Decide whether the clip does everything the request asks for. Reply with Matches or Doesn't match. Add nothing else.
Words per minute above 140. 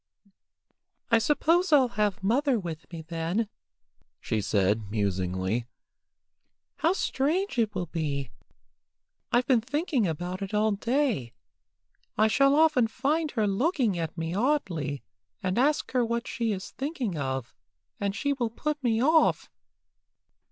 Doesn't match